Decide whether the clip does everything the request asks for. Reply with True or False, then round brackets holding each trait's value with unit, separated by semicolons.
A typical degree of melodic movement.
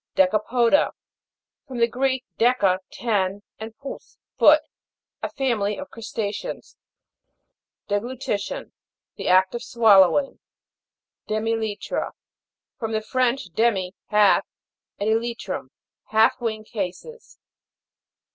True (3.0 semitones)